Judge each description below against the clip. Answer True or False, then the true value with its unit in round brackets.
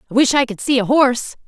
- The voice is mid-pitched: False (250 Hz)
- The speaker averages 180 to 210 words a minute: False (285 wpm)